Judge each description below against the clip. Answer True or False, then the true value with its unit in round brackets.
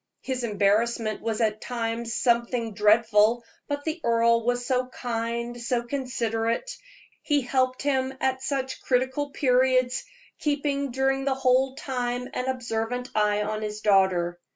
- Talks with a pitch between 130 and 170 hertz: False (245 Hz)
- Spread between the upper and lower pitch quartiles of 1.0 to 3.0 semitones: True (2.5 semitones)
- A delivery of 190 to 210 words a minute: False (135 wpm)